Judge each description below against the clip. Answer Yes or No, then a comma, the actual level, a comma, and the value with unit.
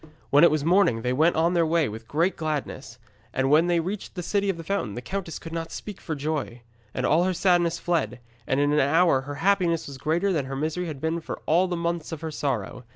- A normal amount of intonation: Yes, average, 3.7 semitones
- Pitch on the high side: No, medium, 160 Hz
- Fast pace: Yes, fast, 245 wpm